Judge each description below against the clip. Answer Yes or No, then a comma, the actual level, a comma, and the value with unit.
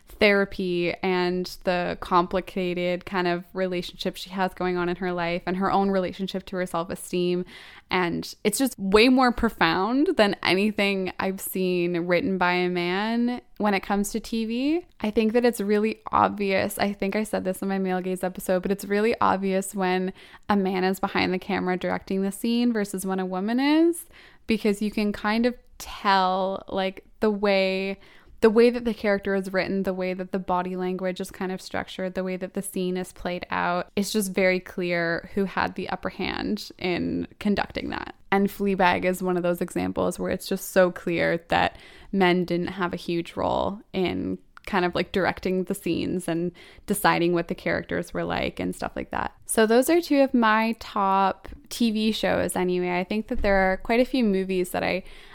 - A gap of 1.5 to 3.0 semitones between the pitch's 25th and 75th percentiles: Yes, narrow, 2.4 semitones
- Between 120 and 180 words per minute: No, average, 195 wpm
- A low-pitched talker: No, high, 190 Hz